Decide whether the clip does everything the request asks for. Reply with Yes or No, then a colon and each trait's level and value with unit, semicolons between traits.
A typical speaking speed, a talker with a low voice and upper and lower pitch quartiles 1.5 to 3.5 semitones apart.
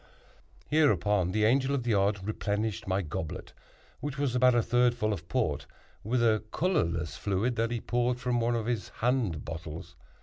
No: average, 175 wpm; low, 115 Hz; average, 4.2 semitones